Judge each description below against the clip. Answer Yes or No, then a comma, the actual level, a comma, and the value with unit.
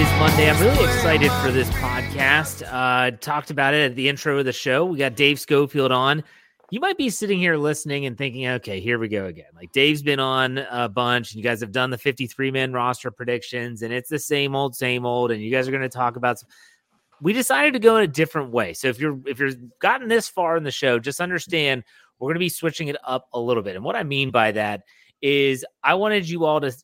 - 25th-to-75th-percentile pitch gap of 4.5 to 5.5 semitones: No, average, 3.5 semitones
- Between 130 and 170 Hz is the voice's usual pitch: Yes, low, 135 Hz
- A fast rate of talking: Yes, fast, 240 wpm